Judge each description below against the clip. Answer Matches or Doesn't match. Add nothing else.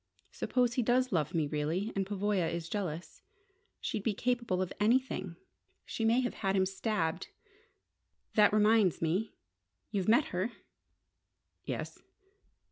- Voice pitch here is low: Doesn't match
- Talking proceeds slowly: Matches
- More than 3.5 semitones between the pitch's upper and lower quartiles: Matches